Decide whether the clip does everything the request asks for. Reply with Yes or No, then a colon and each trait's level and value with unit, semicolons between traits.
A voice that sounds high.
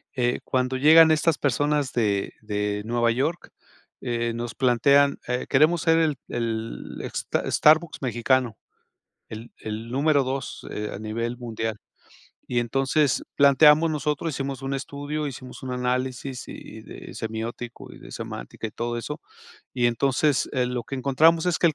No: low, 130 Hz